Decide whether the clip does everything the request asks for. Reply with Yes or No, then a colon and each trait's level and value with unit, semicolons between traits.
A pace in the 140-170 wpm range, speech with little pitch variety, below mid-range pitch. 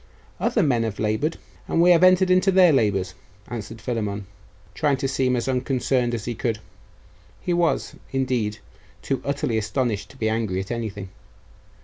No: average, 160 wpm; average, 4.6 semitones; low, 120 Hz